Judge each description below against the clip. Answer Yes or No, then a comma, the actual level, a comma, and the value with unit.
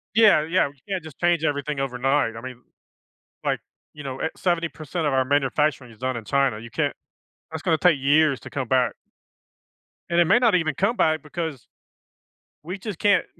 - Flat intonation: No, average, 4.5 semitones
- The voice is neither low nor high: Yes, medium, 150 Hz